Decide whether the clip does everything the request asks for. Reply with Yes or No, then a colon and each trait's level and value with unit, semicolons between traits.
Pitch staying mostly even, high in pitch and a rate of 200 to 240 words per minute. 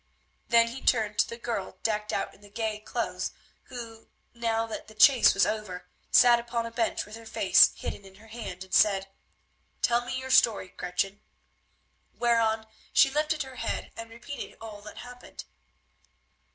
No: narrow, 2.2 semitones; high, 225 Hz; average, 170 wpm